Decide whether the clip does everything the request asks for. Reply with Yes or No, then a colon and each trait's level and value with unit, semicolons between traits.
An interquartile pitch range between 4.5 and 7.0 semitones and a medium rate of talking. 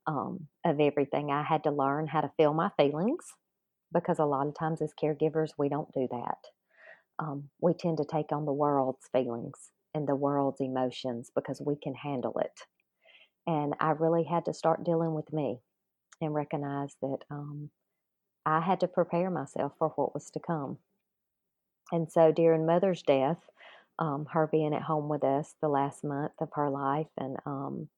No: narrow, 2.4 semitones; average, 180 wpm